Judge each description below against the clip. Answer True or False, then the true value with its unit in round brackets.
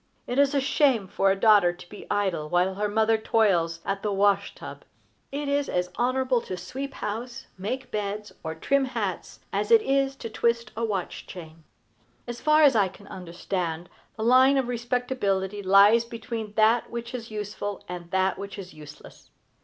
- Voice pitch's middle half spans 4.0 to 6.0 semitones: True (4.5 semitones)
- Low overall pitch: False (210 Hz)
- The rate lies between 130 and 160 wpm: False (180 wpm)